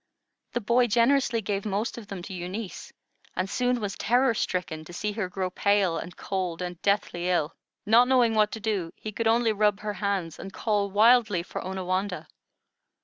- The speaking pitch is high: Yes, high, 205 Hz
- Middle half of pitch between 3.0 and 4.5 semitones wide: Yes, average, 3.5 semitones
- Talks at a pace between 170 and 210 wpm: Yes, average, 185 wpm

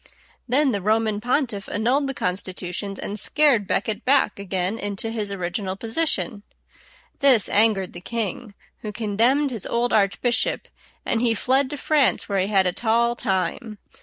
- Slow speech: No, average, 155 wpm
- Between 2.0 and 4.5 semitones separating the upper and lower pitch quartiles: Yes, average, 3.7 semitones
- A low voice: No, high, 220 Hz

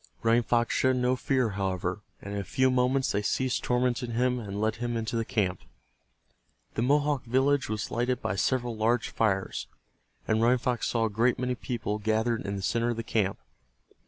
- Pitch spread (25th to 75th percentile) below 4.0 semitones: Yes, narrow, 2.6 semitones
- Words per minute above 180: Yes, average, 190 wpm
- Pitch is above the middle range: No, low, 115 Hz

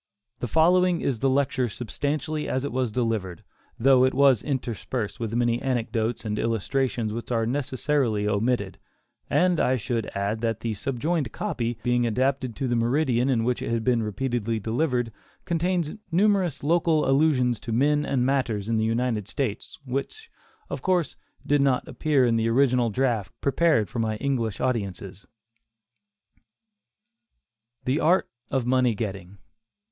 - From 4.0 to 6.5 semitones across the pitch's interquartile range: No, average, 3.5 semitones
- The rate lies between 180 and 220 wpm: No, average, 150 wpm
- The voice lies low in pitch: Yes, low, 125 Hz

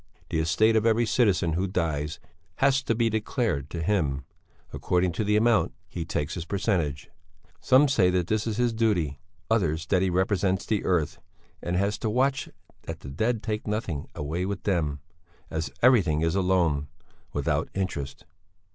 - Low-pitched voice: Yes, very low, 95 Hz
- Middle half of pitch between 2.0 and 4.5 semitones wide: No, average, 5.3 semitones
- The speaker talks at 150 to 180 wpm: Yes, average, 170 wpm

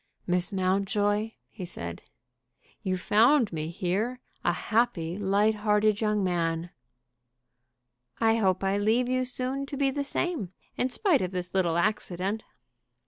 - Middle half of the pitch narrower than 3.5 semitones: No, average, 4.1 semitones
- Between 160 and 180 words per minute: No, average, 140 wpm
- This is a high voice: Yes, high, 205 Hz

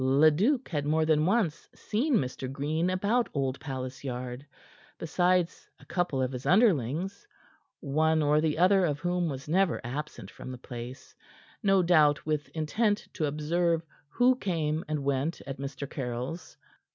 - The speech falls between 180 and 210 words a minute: No, average, 150 wpm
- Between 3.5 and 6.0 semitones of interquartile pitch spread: Yes, average, 4.6 semitones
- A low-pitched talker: No, medium, 155 Hz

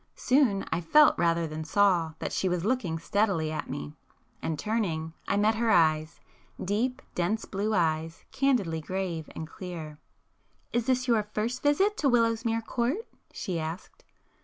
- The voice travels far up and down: Yes, wide, 6.2 semitones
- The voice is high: Yes, high, 195 Hz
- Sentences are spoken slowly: No, average, 145 wpm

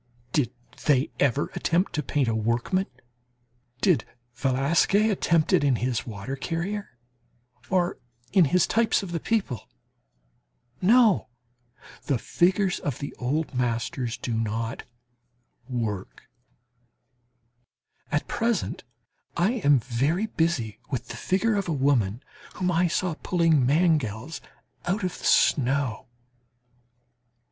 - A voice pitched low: No, medium, 145 Hz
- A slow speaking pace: Yes, slow, 120 wpm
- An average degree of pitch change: No, wide, 6.8 semitones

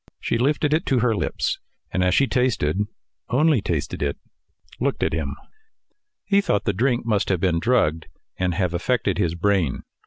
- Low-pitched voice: Yes, low, 100 Hz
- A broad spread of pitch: Yes, wide, 6.6 semitones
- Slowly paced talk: No, average, 175 wpm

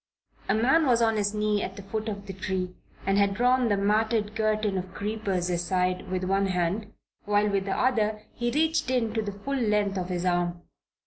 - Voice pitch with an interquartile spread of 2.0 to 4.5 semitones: Yes, average, 2.7 semitones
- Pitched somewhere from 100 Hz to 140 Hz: No, high, 205 Hz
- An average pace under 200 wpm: No, fast, 205 wpm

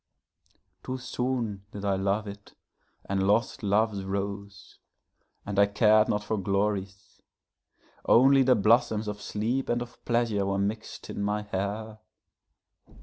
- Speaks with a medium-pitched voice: No, low, 105 Hz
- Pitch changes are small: Yes, narrow, 2.1 semitones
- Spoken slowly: Yes, slow, 130 wpm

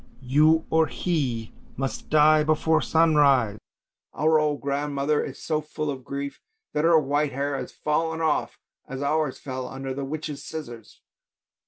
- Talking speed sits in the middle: Yes, average, 150 wpm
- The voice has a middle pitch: Yes, medium, 150 Hz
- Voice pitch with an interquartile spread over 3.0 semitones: No, narrow, 2.4 semitones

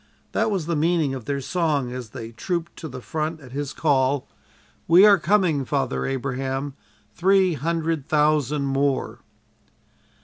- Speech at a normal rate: Yes, average, 145 wpm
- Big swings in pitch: No, average, 3.7 semitones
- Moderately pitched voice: Yes, medium, 145 Hz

